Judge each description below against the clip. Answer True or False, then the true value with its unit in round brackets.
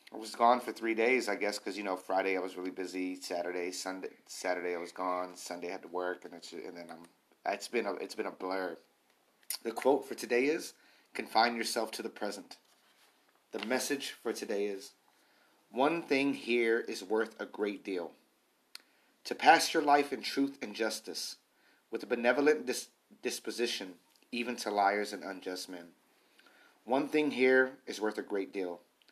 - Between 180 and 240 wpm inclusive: True (185 wpm)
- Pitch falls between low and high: False (105 Hz)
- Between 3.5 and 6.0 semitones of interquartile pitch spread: True (4.7 semitones)